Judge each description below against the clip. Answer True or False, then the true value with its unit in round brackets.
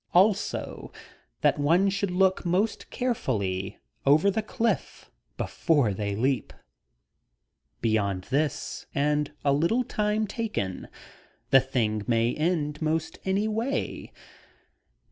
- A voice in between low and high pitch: True (155 Hz)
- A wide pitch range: True (8.4 semitones)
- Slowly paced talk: True (105 wpm)